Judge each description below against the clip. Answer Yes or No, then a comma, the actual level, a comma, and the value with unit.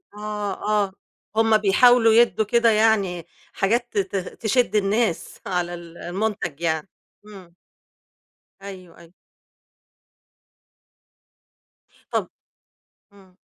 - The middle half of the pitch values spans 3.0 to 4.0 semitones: Yes, average, 3.7 semitones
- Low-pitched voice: No, high, 200 Hz